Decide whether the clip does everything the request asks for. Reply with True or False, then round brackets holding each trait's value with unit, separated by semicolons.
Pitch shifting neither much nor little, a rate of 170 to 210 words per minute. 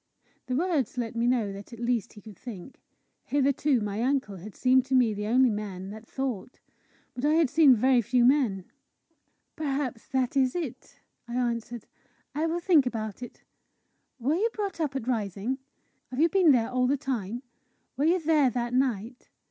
True (3.8 semitones; 180 wpm)